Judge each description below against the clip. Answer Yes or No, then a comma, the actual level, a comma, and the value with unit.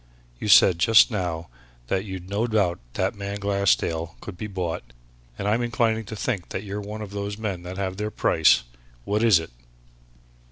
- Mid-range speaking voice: No, low, 100 Hz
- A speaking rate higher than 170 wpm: Yes, average, 185 wpm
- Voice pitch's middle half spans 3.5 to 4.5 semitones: No, narrow, 2.6 semitones